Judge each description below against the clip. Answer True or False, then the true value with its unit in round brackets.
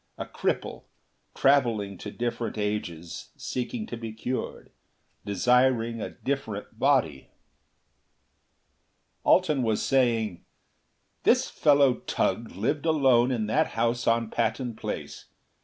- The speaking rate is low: True (105 wpm)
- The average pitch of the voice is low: True (120 Hz)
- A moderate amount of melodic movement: True (3.3 semitones)